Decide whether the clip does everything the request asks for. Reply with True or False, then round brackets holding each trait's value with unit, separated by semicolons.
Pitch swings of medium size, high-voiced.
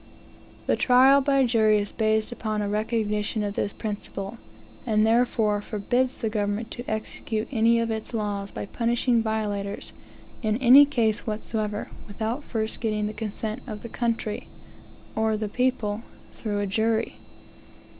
False (1.9 semitones; 220 Hz)